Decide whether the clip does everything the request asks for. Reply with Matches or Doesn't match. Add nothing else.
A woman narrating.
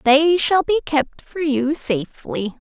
Matches